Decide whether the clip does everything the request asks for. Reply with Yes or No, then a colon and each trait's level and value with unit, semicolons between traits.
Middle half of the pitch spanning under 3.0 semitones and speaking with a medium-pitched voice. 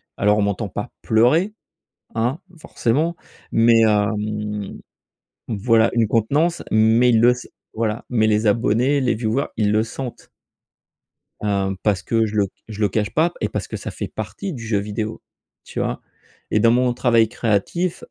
No: narrow, 2.6 semitones; low, 110 Hz